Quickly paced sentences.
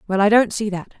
Yes: fast, 300 wpm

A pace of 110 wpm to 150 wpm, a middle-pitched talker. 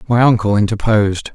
No: slow, 135 wpm; low, 110 Hz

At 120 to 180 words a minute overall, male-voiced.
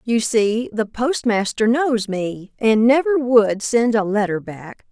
No: average, 160 wpm; female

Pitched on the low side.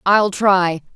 No: high, 190 Hz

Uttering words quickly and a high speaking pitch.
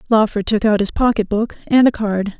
Yes: fast, 225 wpm; high, 215 Hz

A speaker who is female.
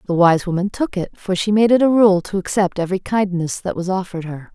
Yes: female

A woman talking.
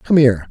No: male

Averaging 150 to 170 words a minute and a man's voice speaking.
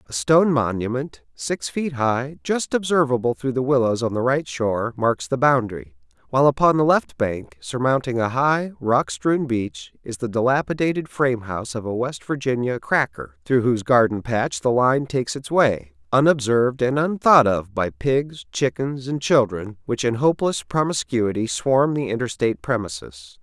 Yes: average, 165 wpm; male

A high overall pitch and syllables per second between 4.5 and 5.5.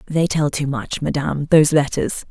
No: medium, 145 Hz; 5.2 syllables/s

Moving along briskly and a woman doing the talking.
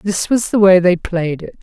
Yes: fast, 260 wpm; female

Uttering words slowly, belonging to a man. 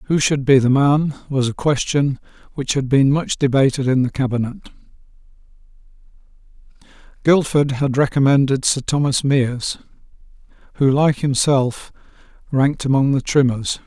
Yes: slow, 125 wpm; male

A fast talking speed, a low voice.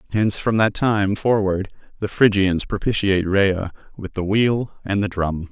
No: average, 165 wpm; low, 100 Hz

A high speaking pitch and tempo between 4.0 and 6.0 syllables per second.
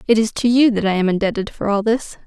No: high, 215 Hz; 6.3 syllables/s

